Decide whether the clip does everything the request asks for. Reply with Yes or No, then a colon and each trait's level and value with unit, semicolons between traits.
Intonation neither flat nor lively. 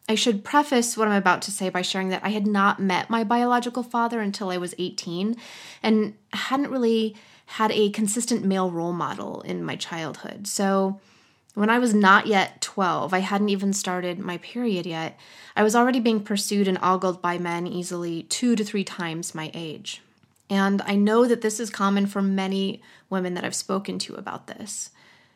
Yes: average, 3.1 semitones